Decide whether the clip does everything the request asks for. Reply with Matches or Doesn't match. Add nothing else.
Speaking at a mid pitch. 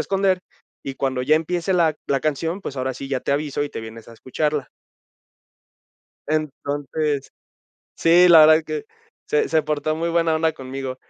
Matches